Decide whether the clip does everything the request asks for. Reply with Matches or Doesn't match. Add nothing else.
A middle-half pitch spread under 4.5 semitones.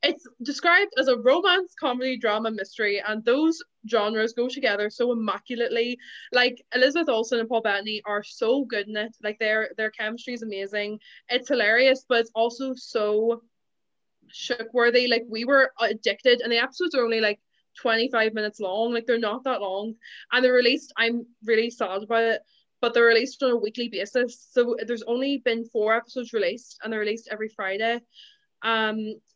Matches